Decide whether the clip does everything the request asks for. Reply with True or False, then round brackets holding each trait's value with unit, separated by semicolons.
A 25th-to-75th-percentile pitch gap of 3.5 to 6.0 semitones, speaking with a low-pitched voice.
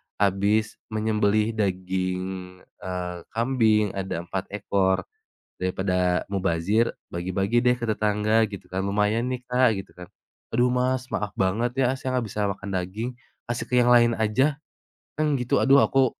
True (4.1 semitones; 105 Hz)